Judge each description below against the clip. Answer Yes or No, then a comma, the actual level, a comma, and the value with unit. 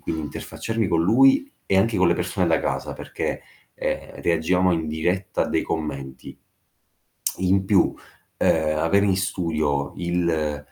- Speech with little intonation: No, average, 3.3 semitones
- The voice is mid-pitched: No, very low, 85 Hz